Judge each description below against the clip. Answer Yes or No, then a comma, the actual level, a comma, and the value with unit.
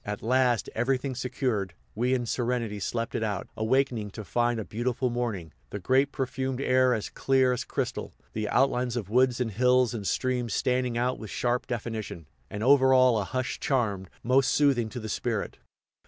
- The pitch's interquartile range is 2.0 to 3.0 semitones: Yes, average, 2.7 semitones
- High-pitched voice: No, low, 120 Hz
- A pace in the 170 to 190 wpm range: Yes, average, 180 wpm